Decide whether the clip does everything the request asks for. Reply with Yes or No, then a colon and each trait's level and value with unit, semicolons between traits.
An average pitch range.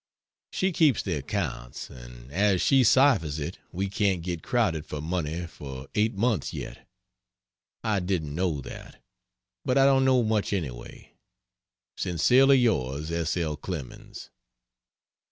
No: wide, 6.7 semitones